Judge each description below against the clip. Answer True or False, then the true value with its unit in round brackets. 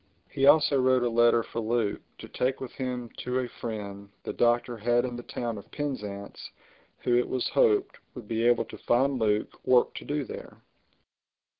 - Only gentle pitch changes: True (2.1 semitones)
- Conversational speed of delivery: True (185 wpm)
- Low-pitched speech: True (120 Hz)